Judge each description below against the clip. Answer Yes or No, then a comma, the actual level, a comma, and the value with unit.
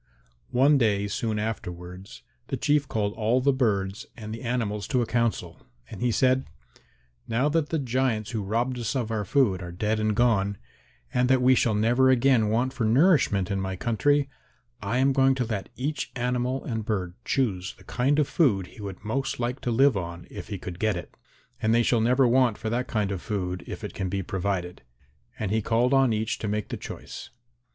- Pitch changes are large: No, average, 4.1 semitones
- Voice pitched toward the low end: Yes, low, 115 Hz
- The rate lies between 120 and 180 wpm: No, fast, 205 wpm